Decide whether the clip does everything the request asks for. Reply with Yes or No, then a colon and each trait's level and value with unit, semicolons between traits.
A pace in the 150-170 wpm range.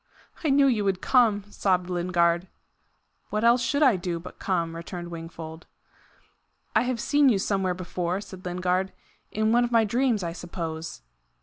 Yes: average, 165 wpm